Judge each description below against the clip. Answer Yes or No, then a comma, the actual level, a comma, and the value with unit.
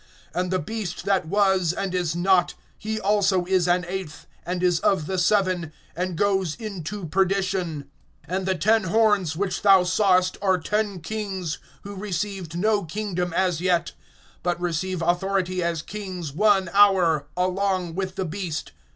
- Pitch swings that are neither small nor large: No, narrow, 2.1 semitones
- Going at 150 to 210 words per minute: Yes, average, 155 wpm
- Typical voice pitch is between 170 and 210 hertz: Yes, medium, 185 Hz